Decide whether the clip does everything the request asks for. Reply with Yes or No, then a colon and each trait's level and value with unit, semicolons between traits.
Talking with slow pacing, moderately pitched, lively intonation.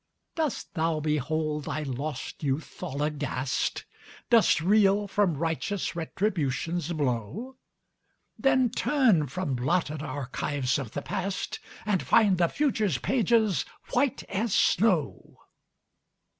Yes: slow, 110 wpm; medium, 165 Hz; wide, 6.3 semitones